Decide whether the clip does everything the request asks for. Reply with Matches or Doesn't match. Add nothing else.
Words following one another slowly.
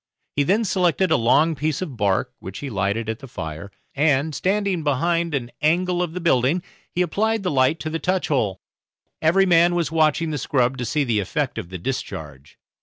Doesn't match